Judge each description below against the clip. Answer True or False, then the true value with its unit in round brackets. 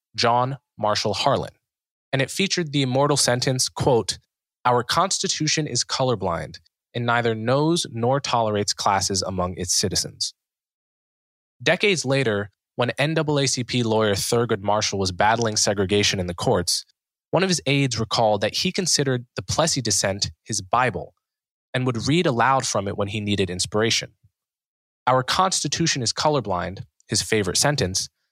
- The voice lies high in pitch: False (120 Hz)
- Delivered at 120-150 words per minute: True (140 wpm)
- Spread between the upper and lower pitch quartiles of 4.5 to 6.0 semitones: True (5.1 semitones)